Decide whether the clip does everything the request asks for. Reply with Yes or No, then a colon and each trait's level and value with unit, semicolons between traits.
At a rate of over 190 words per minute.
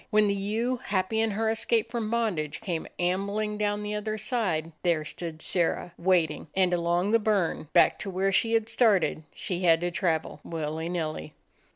No: average, 180 wpm